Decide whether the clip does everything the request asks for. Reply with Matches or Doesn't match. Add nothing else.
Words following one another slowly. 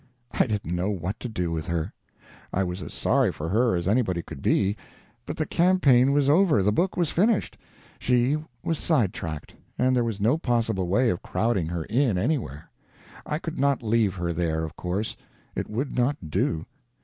Doesn't match